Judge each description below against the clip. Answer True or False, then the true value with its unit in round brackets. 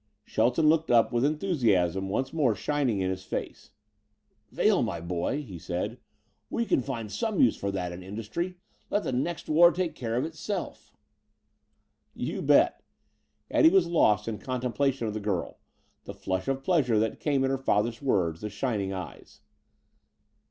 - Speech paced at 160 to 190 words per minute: True (165 wpm)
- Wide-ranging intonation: True (6.8 semitones)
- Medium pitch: False (120 Hz)